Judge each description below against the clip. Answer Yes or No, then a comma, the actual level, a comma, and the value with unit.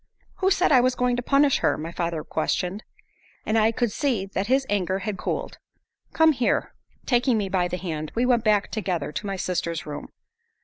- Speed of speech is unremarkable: Yes, average, 195 wpm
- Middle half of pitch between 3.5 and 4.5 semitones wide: No, wide, 5.6 semitones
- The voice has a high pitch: Yes, high, 210 Hz